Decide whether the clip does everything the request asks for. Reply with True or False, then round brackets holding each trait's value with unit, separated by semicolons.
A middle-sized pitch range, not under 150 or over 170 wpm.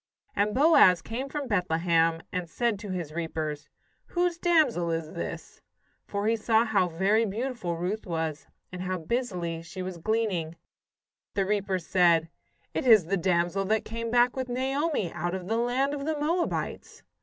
False (5.9 semitones; 165 wpm)